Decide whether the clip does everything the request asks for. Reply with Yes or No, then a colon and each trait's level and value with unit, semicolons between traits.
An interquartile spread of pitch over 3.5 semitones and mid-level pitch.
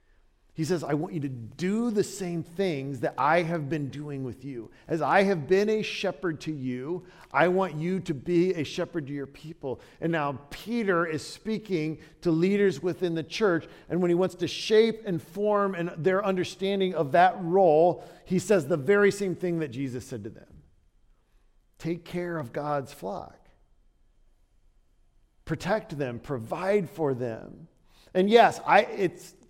Yes: average, 3.9 semitones; medium, 170 Hz